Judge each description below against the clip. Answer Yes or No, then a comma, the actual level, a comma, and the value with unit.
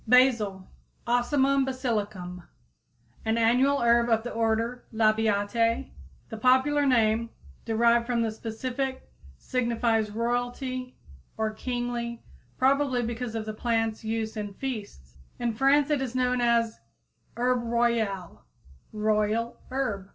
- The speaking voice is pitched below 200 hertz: No, high, 235 Hz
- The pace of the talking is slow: Yes, slow, 120 wpm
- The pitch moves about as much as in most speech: No, narrow, 2.3 semitones